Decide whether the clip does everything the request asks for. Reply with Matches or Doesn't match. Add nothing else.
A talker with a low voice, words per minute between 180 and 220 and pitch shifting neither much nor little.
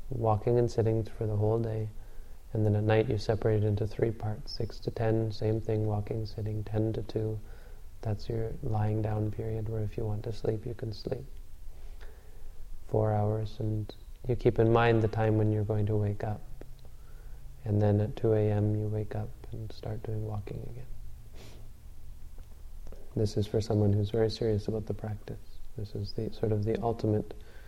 Doesn't match